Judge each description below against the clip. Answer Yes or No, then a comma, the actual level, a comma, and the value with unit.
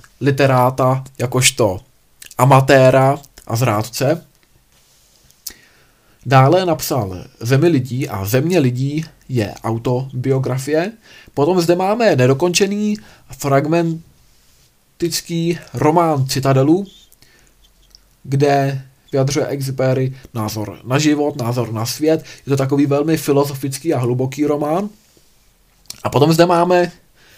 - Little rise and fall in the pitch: No, average, 4.0 semitones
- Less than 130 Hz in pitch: No, low, 135 Hz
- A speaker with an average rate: No, slow, 90 wpm